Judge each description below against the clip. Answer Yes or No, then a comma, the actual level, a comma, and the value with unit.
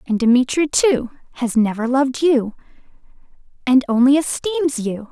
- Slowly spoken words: Yes, slow, 130 wpm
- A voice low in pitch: No, very high, 260 Hz